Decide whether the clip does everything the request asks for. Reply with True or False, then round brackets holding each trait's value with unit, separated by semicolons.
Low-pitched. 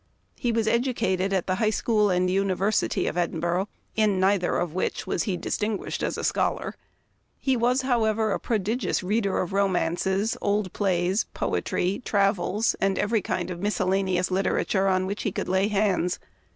False (195 Hz)